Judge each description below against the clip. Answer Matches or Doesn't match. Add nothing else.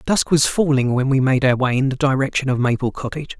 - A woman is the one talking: Doesn't match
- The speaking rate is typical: Doesn't match